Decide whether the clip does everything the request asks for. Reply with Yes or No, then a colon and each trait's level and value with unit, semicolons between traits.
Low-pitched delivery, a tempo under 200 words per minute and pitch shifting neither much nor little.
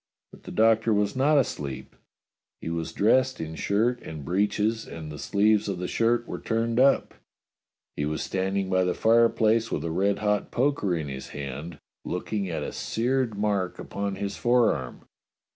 Yes: low, 100 Hz; average, 175 wpm; average, 4.8 semitones